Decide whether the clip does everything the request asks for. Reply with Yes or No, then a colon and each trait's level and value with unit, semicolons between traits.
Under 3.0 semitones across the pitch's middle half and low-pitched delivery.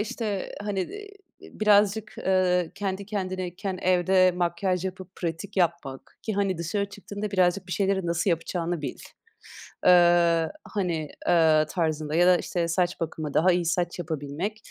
No: narrow, 2.6 semitones; medium, 180 Hz